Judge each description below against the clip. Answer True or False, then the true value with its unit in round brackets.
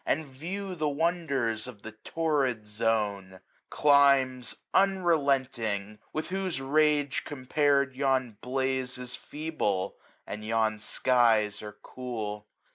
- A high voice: False (130 Hz)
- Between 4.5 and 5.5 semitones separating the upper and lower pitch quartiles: True (5.0 semitones)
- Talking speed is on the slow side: True (110 wpm)